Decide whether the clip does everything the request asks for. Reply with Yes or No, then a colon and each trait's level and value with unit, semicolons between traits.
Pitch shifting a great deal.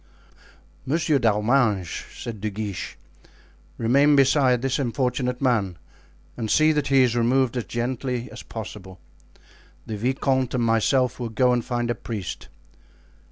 No: average, 2.9 semitones